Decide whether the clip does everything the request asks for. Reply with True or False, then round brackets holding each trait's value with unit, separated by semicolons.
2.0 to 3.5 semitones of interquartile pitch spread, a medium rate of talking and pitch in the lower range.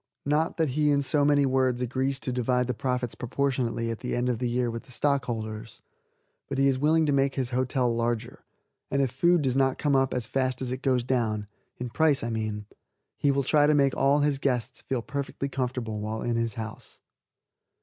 False (2.6 semitones; 210 wpm; 130 Hz)